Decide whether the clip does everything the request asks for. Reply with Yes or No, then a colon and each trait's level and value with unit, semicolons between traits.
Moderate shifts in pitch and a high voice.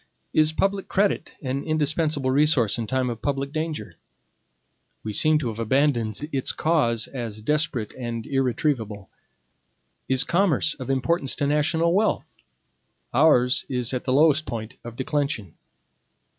No: average, 4.5 semitones; low, 135 Hz